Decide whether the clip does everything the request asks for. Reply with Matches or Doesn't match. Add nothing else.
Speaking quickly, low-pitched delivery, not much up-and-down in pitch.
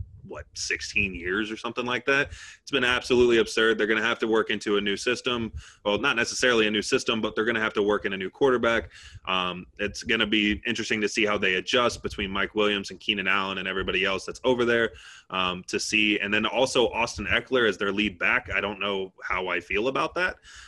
Matches